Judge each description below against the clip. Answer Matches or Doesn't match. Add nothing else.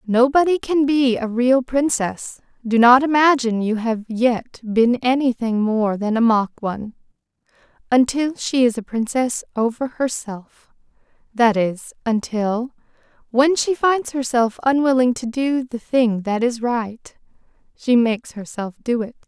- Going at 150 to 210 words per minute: Doesn't match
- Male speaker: Doesn't match